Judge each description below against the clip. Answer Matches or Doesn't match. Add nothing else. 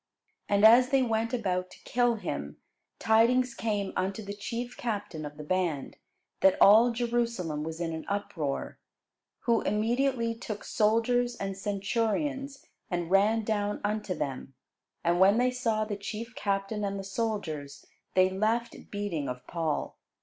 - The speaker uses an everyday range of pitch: Matches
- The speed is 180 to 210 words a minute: Doesn't match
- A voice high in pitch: Matches